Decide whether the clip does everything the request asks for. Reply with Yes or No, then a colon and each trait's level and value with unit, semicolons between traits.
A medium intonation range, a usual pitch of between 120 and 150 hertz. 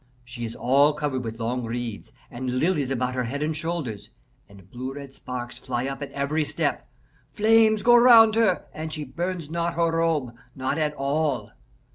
Yes: average, 4.7 semitones; medium, 140 Hz